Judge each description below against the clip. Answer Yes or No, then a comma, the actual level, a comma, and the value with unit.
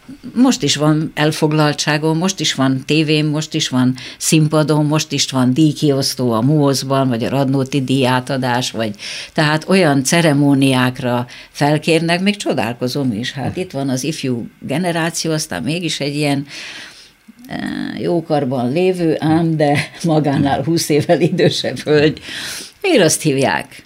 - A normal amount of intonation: Yes, average, 3.0 semitones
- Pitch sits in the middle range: Yes, medium, 150 Hz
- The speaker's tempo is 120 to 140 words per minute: Yes, average, 130 wpm